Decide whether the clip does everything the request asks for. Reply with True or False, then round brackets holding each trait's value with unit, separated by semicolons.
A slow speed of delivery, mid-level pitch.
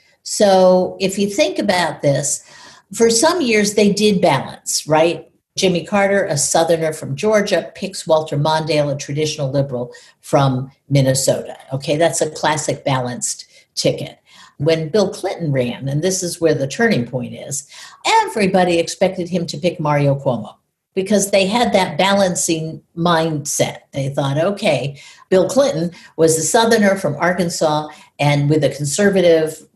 False (145 wpm; 165 Hz)